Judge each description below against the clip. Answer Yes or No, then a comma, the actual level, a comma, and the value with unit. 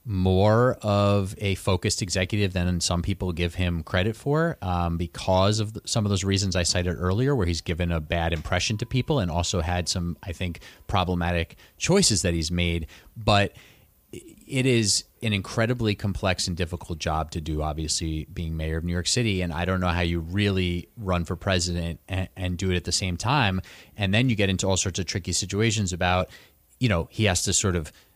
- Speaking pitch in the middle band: No, very low, 95 Hz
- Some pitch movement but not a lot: Yes, average, 3.0 semitones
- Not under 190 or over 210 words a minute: Yes, fast, 205 wpm